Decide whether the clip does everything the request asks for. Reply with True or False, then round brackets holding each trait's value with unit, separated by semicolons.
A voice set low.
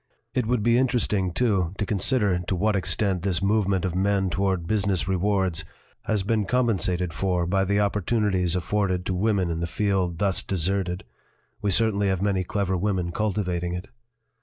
True (95 Hz)